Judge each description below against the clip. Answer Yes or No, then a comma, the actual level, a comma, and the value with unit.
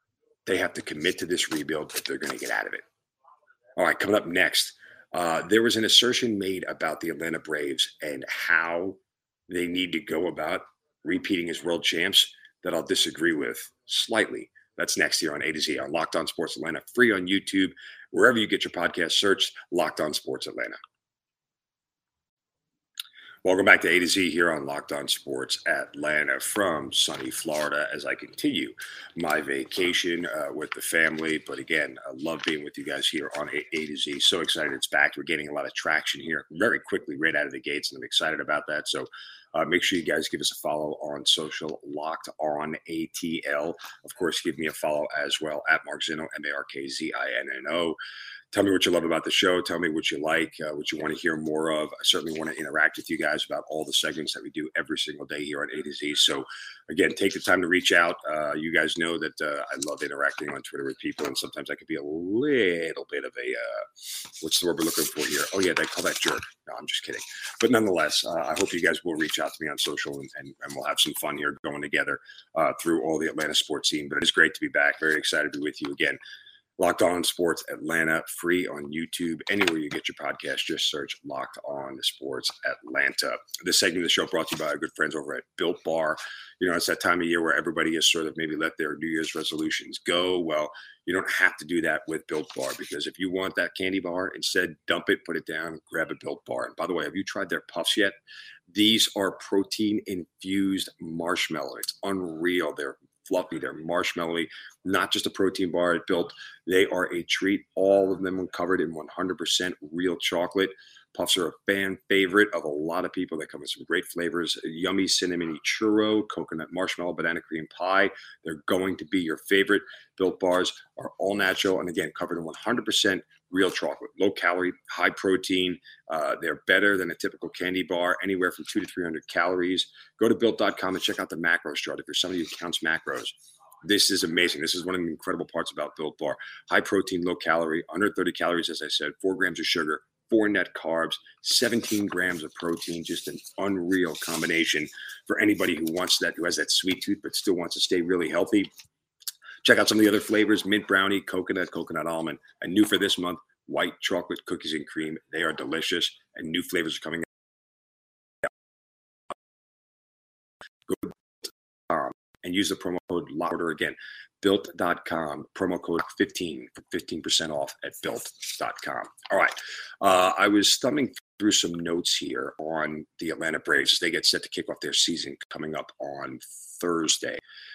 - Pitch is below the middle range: Yes, very low, 95 Hz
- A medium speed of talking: No, fast, 215 wpm